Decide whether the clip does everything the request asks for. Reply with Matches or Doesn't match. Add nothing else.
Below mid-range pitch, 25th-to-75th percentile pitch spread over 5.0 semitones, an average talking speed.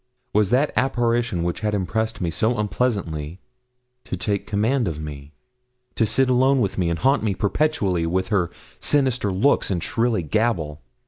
Matches